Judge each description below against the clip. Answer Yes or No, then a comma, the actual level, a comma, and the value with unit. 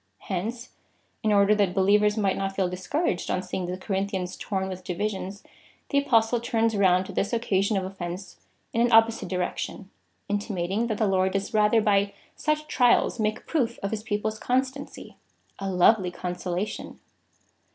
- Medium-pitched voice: No, high, 200 Hz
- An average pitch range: Yes, average, 3.0 semitones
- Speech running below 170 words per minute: Yes, average, 160 wpm